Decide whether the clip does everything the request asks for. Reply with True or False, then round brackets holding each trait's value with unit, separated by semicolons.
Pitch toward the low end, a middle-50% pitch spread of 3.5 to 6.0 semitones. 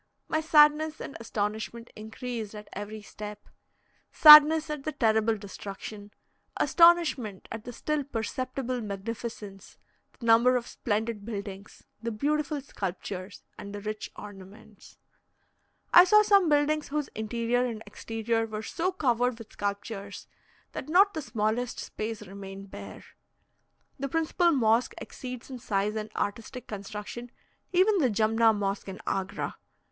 False (225 Hz; 5.0 semitones)